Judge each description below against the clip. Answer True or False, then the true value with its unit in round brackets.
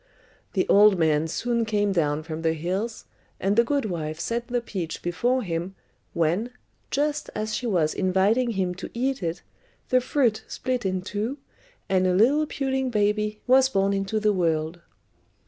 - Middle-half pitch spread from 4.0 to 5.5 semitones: True (5.2 semitones)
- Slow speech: False (165 wpm)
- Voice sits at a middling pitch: False (205 Hz)